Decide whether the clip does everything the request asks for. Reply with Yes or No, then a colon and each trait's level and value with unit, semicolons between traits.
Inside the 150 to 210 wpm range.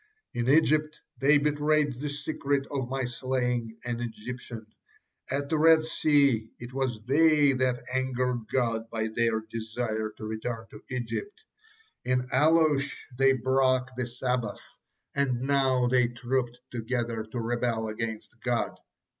No: slow, 135 wpm